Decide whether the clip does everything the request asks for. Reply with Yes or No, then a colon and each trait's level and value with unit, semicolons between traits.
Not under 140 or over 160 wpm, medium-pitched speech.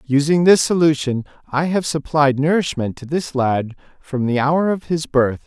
No: average, 175 wpm; medium, 145 Hz